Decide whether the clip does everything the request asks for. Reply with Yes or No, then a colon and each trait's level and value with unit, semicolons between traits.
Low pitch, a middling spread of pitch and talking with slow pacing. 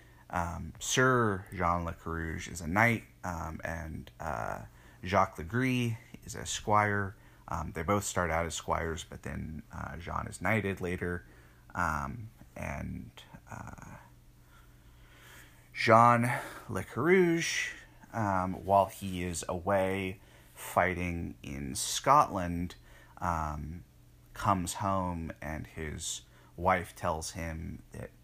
Yes: very low, 90 Hz; average, 4.3 semitones; slow, 115 wpm